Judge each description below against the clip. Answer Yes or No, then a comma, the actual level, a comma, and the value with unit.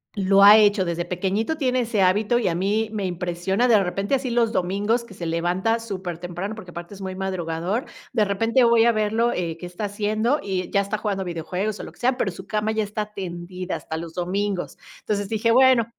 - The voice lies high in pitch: Yes, high, 200 Hz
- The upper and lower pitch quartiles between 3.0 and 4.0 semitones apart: Yes, average, 3.5 semitones